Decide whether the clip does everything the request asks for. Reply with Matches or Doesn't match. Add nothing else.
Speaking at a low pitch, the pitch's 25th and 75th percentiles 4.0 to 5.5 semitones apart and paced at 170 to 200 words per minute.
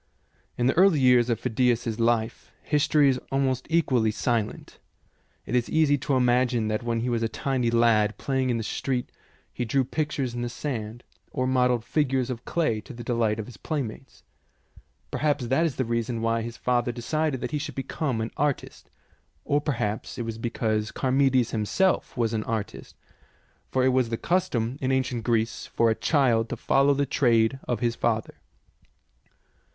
Doesn't match